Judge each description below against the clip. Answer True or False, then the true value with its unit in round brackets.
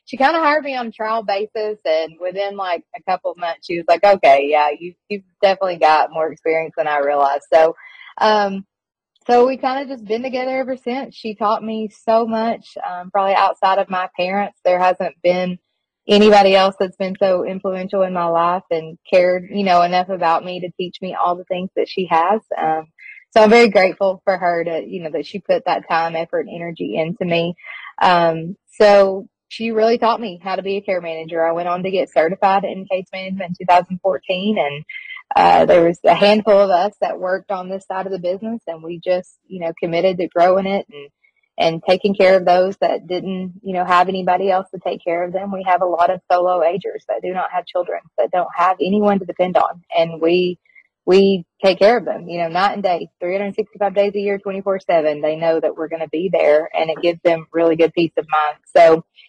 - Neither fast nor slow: False (225 wpm)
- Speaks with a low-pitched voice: False (185 Hz)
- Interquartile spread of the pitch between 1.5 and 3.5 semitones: True (2.9 semitones)